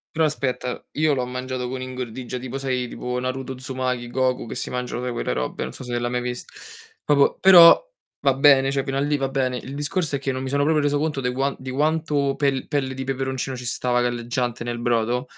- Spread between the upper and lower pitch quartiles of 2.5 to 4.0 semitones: No, narrow, 2.0 semitones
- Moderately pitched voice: No, low, 130 Hz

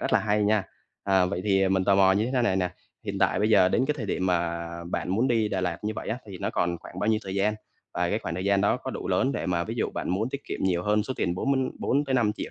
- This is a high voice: No, low, 100 Hz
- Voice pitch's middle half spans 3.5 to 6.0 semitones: No, average, 3.0 semitones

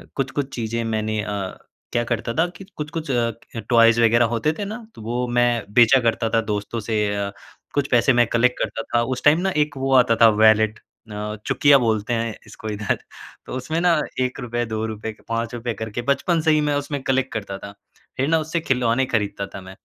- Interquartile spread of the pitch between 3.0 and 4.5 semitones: Yes, average, 3.4 semitones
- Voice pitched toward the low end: Yes, low, 115 Hz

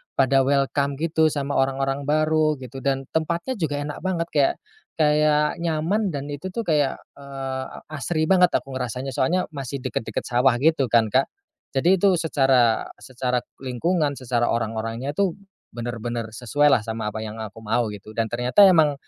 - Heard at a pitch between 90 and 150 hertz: Yes, low, 135 Hz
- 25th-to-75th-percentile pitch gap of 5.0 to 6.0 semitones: No, average, 4.0 semitones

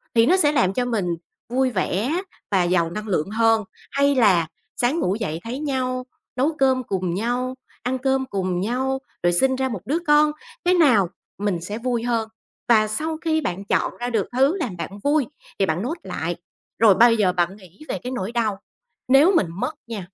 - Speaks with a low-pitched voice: No, high, 235 Hz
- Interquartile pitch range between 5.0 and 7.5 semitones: Yes, wide, 5.4 semitones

